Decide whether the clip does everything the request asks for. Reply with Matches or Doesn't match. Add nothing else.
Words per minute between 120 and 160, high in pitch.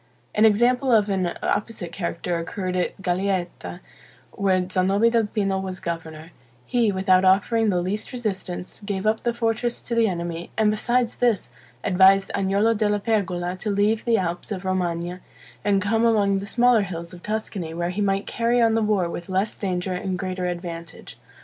Doesn't match